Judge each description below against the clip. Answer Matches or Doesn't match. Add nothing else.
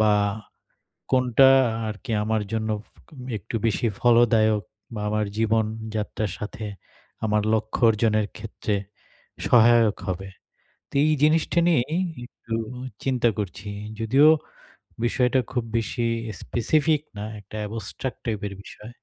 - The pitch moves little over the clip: Matches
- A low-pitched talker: Matches